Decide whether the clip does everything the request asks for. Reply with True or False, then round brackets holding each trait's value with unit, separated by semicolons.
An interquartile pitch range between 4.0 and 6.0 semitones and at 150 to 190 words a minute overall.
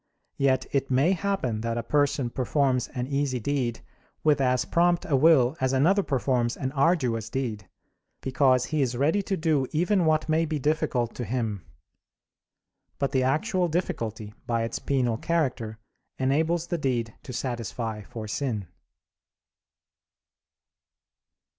False (4.6 semitones; 140 wpm)